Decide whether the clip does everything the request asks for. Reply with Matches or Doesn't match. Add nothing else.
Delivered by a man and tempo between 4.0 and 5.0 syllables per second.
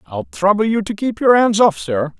Matches